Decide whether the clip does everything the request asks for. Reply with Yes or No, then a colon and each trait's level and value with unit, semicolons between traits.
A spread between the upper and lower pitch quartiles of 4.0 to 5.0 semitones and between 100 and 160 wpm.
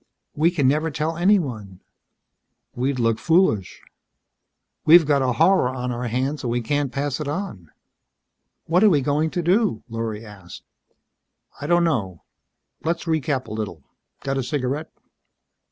No: wide, 5.5 semitones; average, 150 wpm